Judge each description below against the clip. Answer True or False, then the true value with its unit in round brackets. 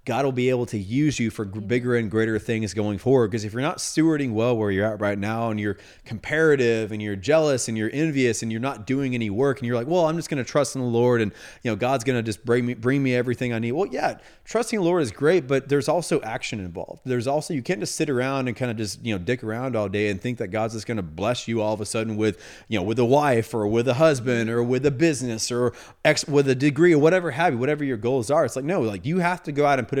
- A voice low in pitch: True (125 Hz)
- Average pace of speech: False (290 wpm)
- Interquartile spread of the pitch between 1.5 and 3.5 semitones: False (4.2 semitones)